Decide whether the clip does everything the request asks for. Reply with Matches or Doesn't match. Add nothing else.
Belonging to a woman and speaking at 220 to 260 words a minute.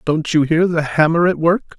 Doesn't match